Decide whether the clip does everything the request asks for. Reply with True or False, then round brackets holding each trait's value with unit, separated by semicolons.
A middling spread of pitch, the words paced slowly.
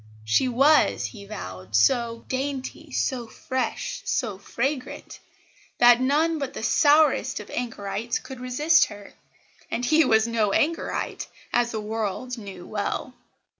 True (4.0 semitones; 130 wpm)